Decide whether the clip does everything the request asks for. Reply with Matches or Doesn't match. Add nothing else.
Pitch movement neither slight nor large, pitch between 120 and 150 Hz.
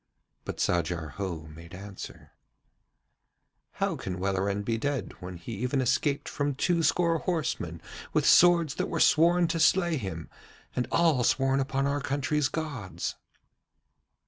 Doesn't match